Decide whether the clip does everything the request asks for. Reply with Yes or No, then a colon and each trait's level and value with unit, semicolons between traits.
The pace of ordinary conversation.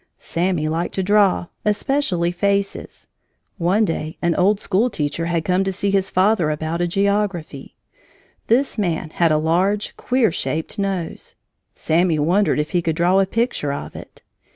Yes: average, 160 wpm